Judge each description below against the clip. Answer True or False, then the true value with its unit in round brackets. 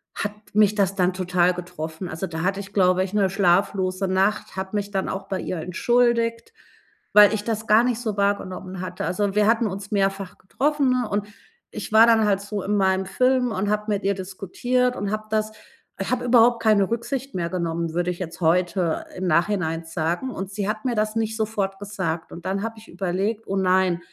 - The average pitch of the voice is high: True (195 Hz)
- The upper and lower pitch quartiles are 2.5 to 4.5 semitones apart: True (2.8 semitones)